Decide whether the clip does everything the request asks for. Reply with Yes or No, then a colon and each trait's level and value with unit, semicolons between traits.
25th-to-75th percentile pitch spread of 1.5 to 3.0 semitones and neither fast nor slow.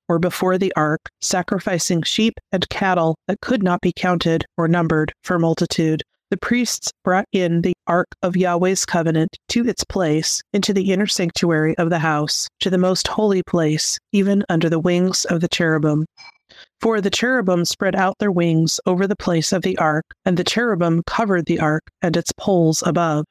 Yes: narrow, 2.5 semitones; average, 185 wpm